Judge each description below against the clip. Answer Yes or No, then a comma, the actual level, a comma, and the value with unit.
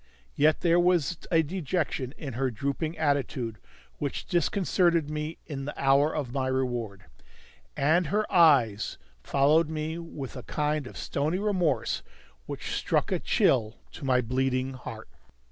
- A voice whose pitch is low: No, medium, 145 Hz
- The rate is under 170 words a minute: Yes, average, 145 wpm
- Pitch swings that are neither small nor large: Yes, average, 3.9 semitones